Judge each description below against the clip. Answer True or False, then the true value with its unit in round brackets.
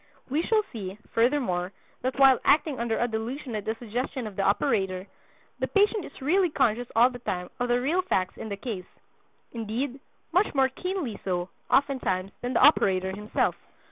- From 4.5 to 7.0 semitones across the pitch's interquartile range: True (5.6 semitones)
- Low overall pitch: False (240 Hz)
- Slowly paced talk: False (175 wpm)